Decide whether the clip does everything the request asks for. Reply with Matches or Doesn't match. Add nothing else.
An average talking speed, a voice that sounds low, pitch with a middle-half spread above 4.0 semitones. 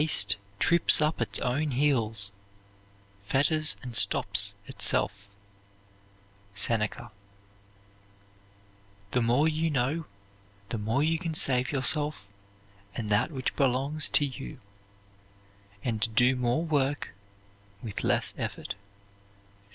Doesn't match